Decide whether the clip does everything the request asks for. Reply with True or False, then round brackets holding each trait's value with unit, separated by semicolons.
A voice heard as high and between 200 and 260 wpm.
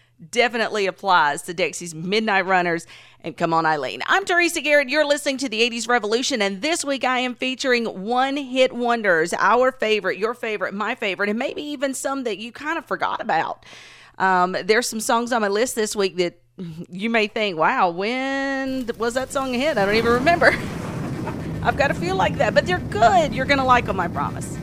True (230 Hz; 205 wpm)